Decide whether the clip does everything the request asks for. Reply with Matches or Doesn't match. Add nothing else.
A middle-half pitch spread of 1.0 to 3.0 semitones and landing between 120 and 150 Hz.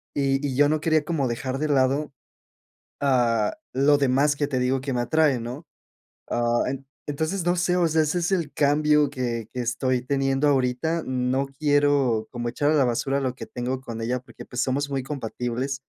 Matches